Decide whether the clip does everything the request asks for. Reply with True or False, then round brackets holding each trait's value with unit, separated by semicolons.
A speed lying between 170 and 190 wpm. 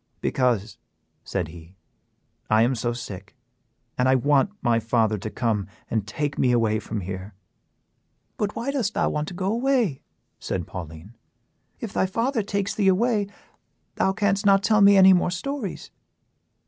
False (160 wpm)